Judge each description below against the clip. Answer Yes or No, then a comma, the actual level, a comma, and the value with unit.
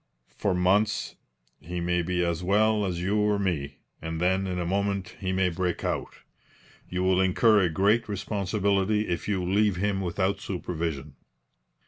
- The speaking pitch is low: Yes, very low, 95 Hz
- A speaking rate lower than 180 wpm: Yes, average, 160 wpm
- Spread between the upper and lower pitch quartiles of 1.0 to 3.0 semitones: Yes, narrow, 2.4 semitones